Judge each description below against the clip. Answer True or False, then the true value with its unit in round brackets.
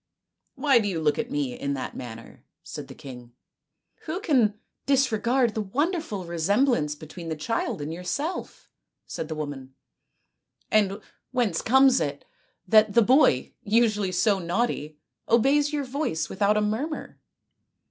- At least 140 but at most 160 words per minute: False (170 wpm)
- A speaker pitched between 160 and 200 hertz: False (210 Hz)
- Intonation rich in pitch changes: True (8.1 semitones)